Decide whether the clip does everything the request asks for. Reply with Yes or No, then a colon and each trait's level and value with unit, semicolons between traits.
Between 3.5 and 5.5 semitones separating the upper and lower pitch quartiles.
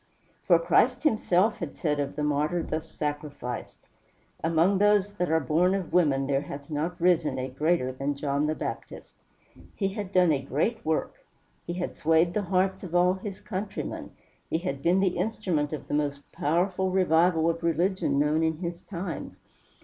Yes: average, 3.9 semitones